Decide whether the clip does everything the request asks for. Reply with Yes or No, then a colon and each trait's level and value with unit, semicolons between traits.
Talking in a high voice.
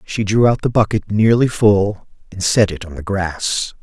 No: low, 105 Hz